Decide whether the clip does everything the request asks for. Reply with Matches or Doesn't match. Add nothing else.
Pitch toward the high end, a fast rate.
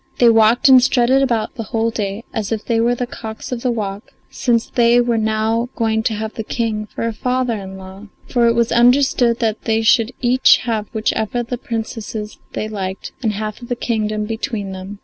Matches